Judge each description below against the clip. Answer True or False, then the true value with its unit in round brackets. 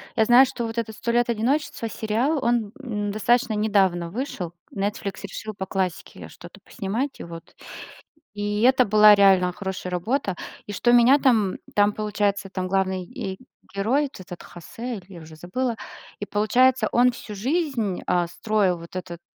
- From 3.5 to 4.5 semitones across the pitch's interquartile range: True (4.0 semitones)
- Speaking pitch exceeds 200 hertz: True (210 Hz)